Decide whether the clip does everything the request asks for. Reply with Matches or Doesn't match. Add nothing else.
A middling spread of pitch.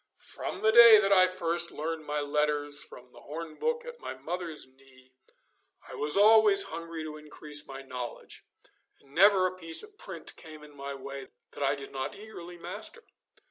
Matches